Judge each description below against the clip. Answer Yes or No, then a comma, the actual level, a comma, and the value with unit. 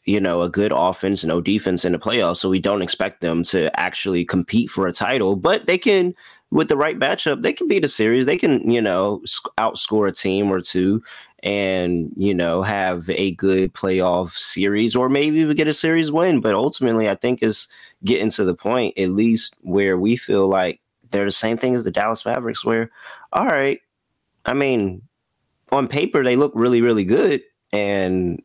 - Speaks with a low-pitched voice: Yes, low, 100 Hz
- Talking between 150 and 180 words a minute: No, average, 195 wpm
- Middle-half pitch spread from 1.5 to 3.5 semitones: No, average, 4.1 semitones